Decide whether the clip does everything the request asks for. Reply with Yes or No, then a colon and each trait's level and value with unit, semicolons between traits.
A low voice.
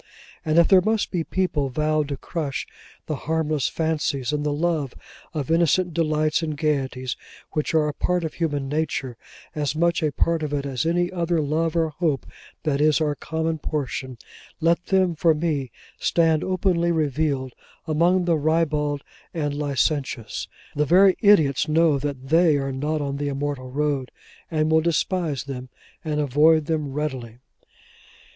No: medium, 155 Hz